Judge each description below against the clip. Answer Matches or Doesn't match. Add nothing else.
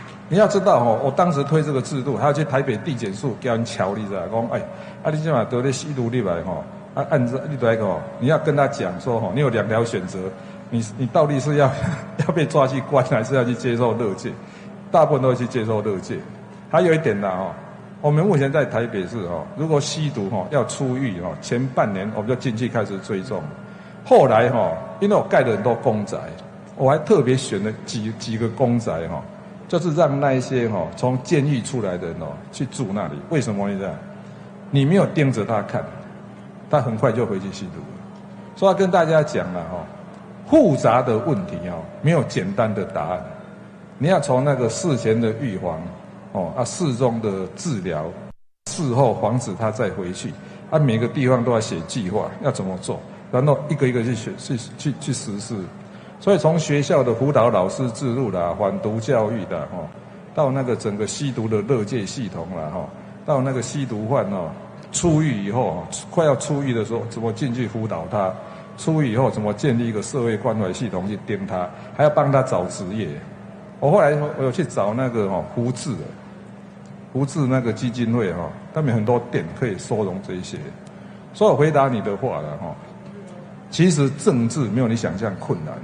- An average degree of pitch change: Matches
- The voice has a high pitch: Doesn't match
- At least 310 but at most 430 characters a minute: Doesn't match